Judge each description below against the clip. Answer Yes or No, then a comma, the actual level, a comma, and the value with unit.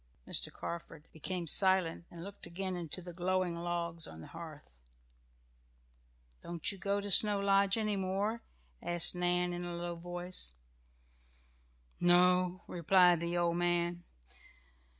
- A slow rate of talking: Yes, slow, 130 wpm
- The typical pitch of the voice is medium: Yes, medium, 175 Hz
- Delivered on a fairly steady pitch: Yes, narrow, 1.6 semitones